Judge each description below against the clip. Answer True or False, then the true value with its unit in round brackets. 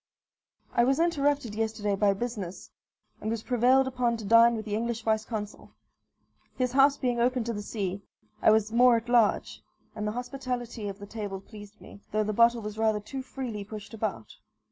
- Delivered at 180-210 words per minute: True (190 wpm)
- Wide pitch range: False (2.7 semitones)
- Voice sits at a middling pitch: False (225 Hz)